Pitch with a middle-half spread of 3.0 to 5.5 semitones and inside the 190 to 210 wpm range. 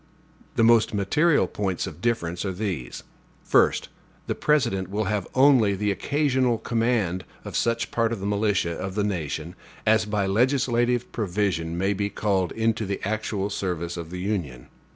No: average, 3.8 semitones; average, 160 wpm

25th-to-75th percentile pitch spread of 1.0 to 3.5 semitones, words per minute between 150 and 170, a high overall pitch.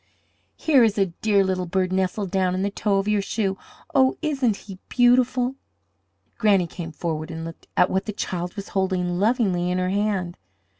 No: average, 3.0 semitones; average, 185 wpm; high, 195 Hz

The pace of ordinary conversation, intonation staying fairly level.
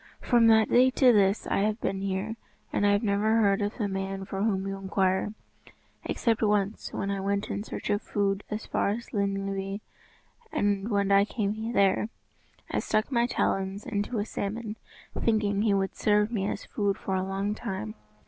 Yes: average, 190 wpm; narrow, 1.7 semitones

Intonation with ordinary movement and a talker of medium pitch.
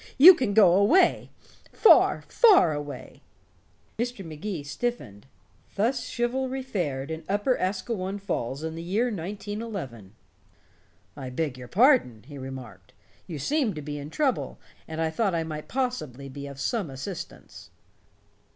No: wide, 8.6 semitones; medium, 175 Hz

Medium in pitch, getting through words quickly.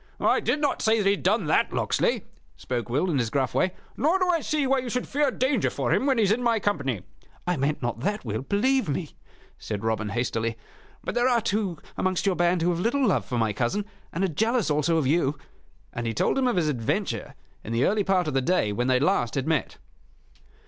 Yes: medium, 175 Hz; fast, 240 wpm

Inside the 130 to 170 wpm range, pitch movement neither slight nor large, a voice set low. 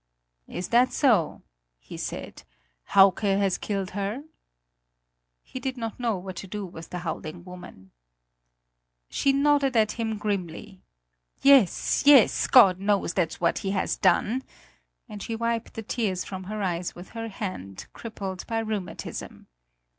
No: average, 145 wpm; average, 3.9 semitones; high, 200 Hz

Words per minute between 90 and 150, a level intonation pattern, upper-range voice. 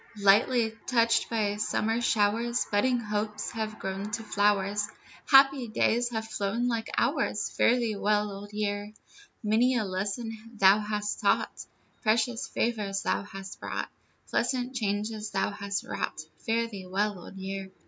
Yes: average, 145 wpm; narrow, 2.3 semitones; high, 210 Hz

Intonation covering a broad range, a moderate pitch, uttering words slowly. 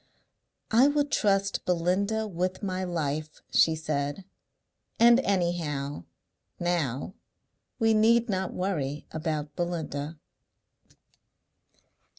No: average, 4.5 semitones; medium, 175 Hz; slow, 90 wpm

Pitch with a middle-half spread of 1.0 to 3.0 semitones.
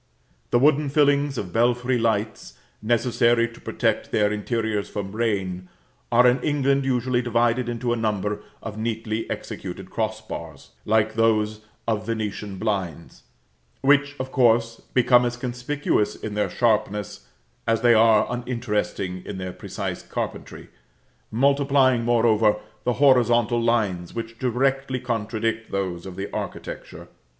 Yes: average, 2.7 semitones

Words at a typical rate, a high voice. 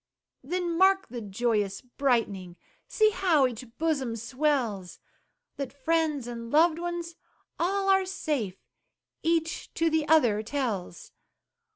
No: slow, 115 wpm; very high, 285 Hz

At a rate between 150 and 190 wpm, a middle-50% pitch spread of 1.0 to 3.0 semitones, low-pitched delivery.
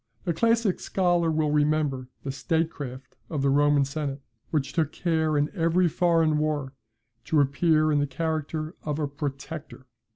No: average, 160 wpm; narrow, 2.4 semitones; medium, 155 Hz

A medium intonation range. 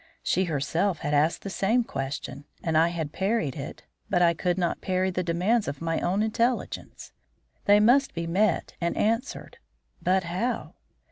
Yes: average, 4.0 semitones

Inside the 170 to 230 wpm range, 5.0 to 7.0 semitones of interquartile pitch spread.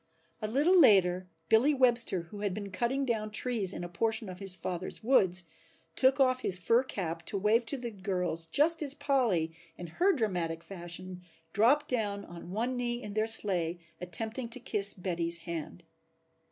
Yes: average, 175 wpm; wide, 5.4 semitones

